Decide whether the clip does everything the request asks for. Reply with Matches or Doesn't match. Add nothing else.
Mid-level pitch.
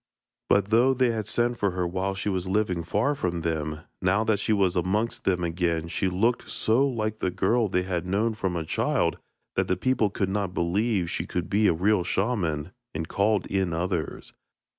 Doesn't match